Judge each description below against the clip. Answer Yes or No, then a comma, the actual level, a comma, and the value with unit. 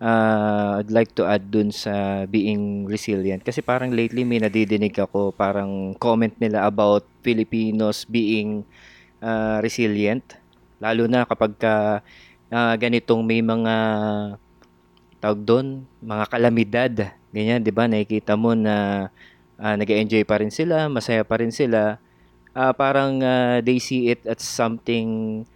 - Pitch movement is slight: Yes, narrow, 1.9 semitones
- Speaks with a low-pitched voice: Yes, low, 110 Hz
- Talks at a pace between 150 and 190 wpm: No, average, 135 wpm